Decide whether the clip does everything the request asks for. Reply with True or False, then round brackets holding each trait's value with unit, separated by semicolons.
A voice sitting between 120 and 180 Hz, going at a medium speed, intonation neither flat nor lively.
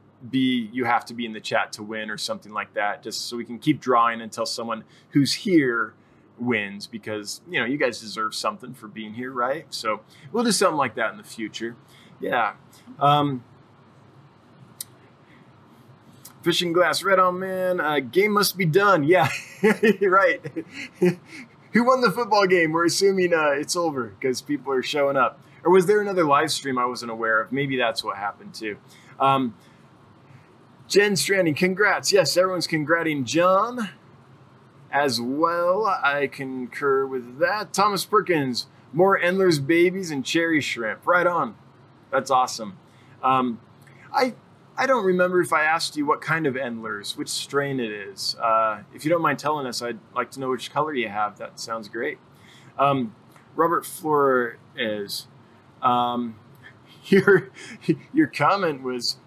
False (140 Hz; 160 wpm; 6.6 semitones)